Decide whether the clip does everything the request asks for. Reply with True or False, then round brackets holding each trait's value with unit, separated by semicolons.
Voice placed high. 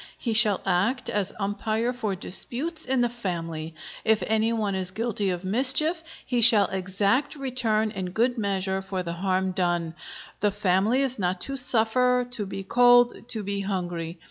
True (210 Hz)